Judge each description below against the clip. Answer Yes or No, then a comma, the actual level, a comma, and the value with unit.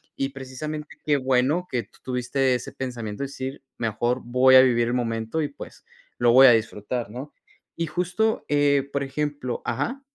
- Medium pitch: No, low, 130 Hz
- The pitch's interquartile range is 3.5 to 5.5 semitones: No, average, 3.1 semitones